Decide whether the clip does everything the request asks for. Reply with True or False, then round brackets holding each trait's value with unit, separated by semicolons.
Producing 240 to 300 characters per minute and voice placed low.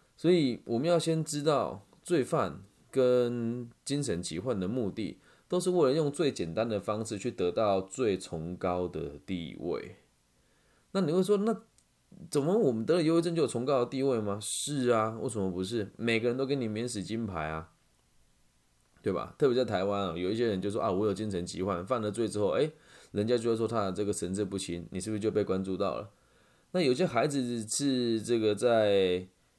True (280 characters per minute; 110 Hz)